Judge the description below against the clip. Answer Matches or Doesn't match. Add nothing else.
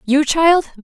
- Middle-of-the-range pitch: Doesn't match